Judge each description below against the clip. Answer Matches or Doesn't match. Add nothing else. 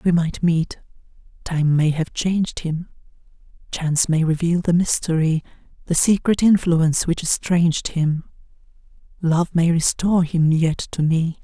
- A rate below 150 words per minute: Matches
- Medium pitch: Matches